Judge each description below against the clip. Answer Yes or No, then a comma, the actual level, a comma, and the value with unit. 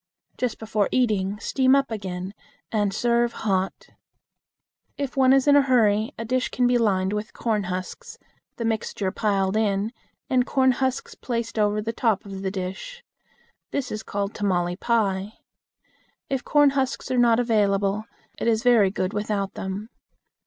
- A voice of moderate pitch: No, high, 220 Hz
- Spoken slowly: No, average, 160 wpm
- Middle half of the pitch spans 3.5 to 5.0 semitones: Yes, average, 3.8 semitones